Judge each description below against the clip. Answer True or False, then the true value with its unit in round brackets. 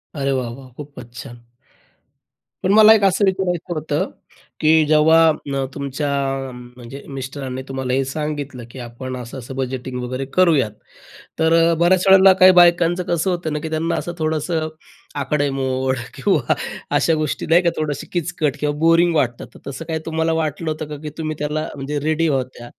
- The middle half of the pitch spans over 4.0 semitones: False (3.7 semitones)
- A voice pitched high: False (150 Hz)